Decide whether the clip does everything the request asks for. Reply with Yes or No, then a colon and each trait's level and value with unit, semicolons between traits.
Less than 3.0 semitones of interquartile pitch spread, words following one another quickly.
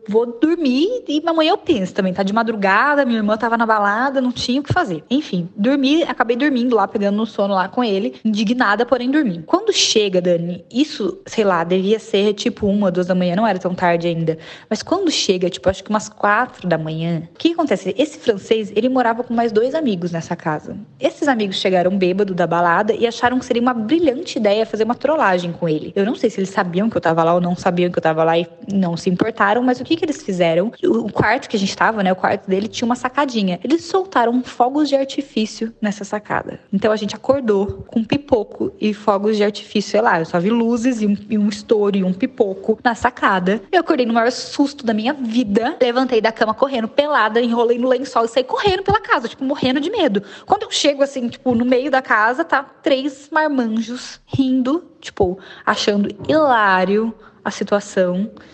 No: average, 5.0 semitones; fast, 215 wpm